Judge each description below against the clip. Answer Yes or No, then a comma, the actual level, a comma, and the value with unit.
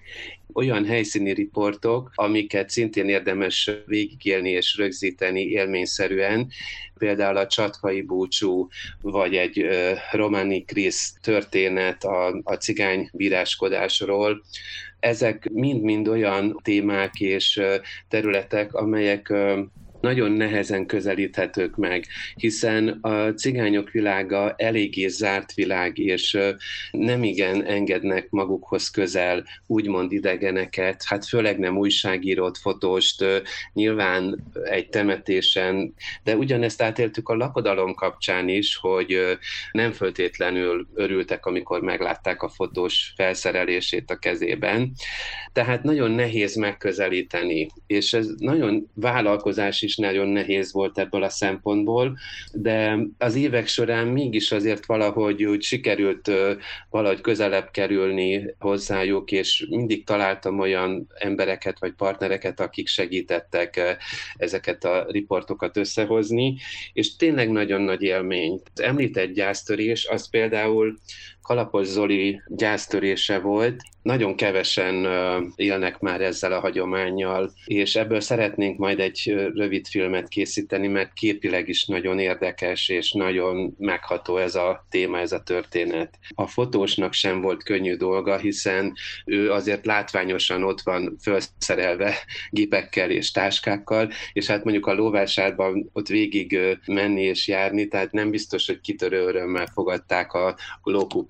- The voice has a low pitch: Yes, low, 100 Hz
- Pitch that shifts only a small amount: Yes, narrow, 2.1 semitones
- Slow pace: No, average, 115 wpm